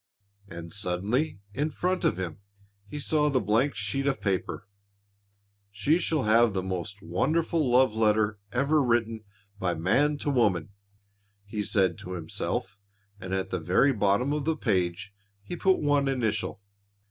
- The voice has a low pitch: Yes, low, 110 Hz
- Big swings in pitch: Yes, wide, 6.8 semitones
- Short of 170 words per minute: Yes, average, 150 wpm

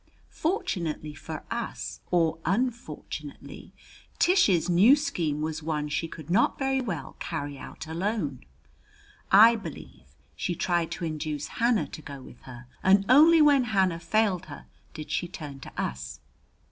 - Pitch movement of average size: No, wide, 6.7 semitones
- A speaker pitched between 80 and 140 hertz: No, medium, 170 Hz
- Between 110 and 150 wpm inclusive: Yes, average, 145 wpm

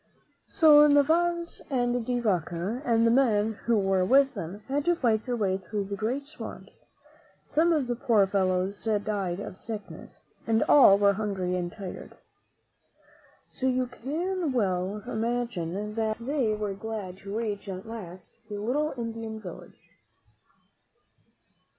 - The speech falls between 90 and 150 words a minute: Yes, average, 140 wpm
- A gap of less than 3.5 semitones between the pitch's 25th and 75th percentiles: No, average, 4.3 semitones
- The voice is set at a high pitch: Yes, high, 220 Hz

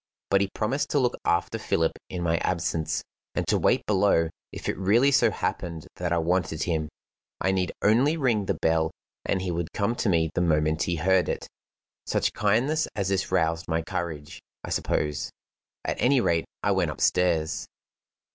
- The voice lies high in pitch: No, very low, 90 Hz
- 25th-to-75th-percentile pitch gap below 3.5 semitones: No, average, 4.2 semitones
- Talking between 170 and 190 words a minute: Yes, average, 180 wpm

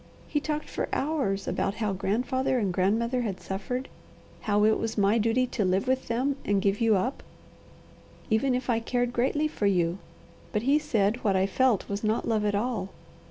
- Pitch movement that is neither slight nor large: Yes, average, 4.1 semitones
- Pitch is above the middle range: Yes, high, 225 Hz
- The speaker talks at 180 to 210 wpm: Yes, average, 190 wpm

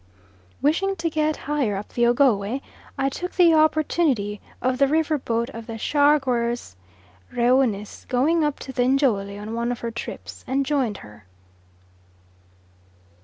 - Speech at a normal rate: Yes, average, 145 wpm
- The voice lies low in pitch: No, very high, 255 Hz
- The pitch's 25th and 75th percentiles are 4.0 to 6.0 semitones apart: Yes, average, 4.5 semitones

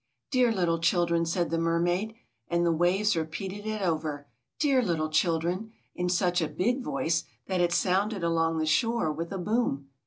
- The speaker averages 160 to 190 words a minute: Yes, average, 175 wpm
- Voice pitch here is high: No, medium, 175 Hz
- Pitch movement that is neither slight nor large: Yes, average, 3.6 semitones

